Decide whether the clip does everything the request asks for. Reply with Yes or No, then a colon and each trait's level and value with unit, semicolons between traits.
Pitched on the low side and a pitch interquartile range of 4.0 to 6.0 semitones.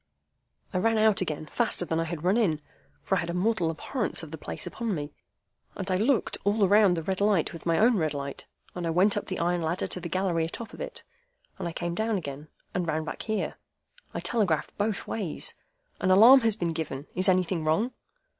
No: medium, 180 Hz; average, 4.5 semitones